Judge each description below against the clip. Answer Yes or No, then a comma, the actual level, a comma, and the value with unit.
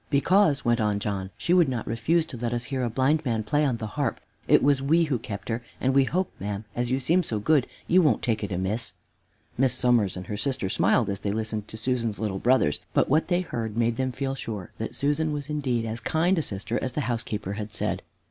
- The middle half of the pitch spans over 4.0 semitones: Yes, average, 4.8 semitones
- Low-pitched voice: Yes, low, 120 Hz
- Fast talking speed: Yes, fast, 240 wpm